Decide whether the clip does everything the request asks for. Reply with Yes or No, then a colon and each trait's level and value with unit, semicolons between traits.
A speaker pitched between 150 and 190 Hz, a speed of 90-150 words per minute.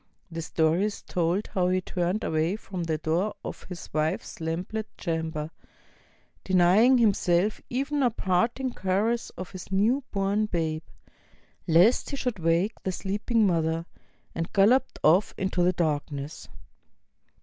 Yes: medium, 185 Hz; average, 140 wpm